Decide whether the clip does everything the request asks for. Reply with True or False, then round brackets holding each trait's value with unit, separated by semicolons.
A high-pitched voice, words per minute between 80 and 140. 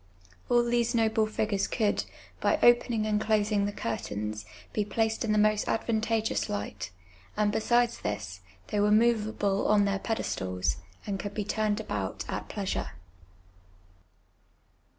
True (210 Hz; 135 wpm)